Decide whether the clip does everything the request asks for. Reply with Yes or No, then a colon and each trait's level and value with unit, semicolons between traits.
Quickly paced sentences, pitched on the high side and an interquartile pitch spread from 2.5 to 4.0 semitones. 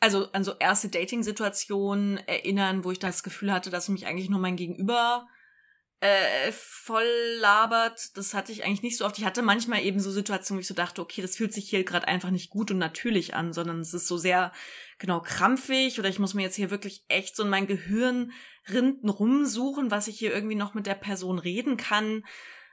Yes: fast, 210 wpm; high, 200 Hz; average, 2.9 semitones